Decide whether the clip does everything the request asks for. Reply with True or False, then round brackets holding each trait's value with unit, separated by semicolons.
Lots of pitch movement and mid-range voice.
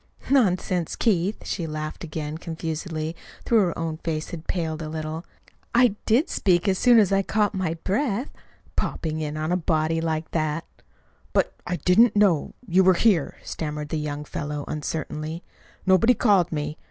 False (3.7 semitones; 165 Hz)